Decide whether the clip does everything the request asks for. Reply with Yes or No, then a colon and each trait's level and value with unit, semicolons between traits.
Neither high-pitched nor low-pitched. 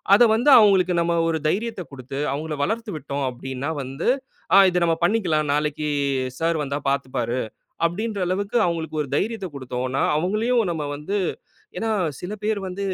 Yes: medium, 165 Hz